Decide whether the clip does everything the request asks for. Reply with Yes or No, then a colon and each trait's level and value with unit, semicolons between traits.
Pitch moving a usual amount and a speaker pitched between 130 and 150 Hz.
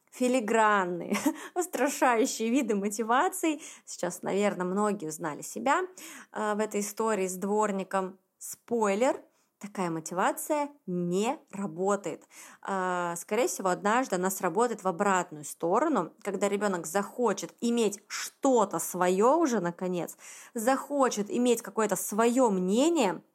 No: average, 5.0 semitones; high, 210 Hz